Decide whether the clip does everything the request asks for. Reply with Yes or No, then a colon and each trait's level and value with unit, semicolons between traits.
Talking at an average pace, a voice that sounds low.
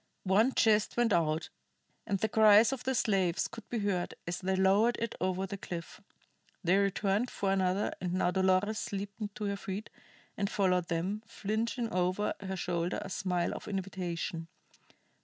No: average, 165 wpm; high, 195 Hz